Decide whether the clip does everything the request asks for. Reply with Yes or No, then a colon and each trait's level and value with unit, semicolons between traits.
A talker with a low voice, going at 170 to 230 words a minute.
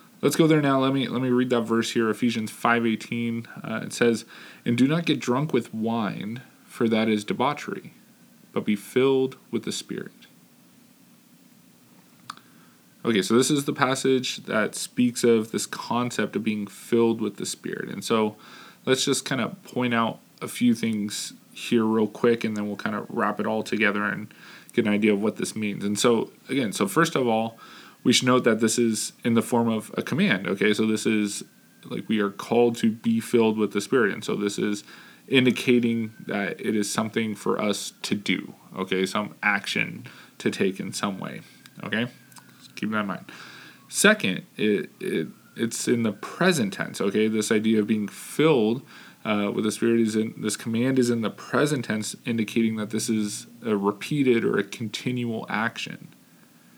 Yes: low, 115 Hz; average, 190 wpm